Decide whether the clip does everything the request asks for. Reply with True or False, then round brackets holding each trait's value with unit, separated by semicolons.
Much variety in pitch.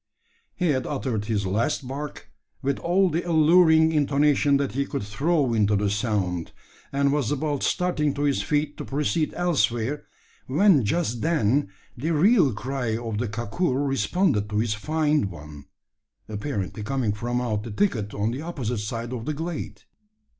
True (5.9 semitones)